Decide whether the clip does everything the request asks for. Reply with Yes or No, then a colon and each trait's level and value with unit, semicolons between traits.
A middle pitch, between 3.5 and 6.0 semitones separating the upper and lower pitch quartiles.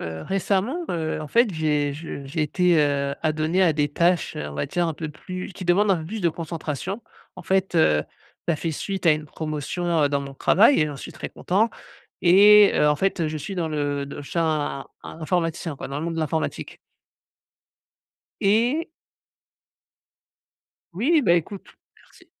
Yes: medium, 165 Hz; average, 4.1 semitones